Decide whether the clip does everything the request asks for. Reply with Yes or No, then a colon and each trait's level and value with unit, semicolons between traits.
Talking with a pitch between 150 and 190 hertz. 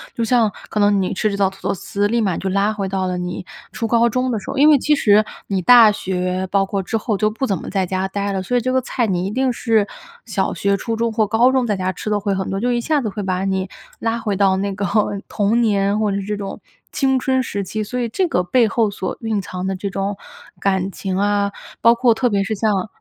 No: high, 205 Hz